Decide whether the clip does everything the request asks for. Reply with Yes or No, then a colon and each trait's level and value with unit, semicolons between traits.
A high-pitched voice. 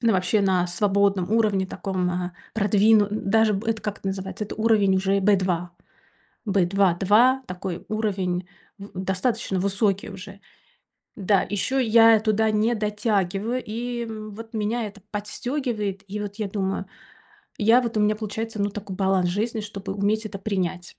Yes: high, 205 Hz